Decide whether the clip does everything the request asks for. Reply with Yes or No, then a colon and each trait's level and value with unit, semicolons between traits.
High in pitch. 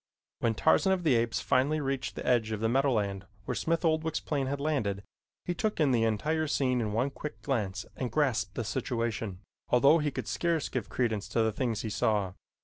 No: low, 125 Hz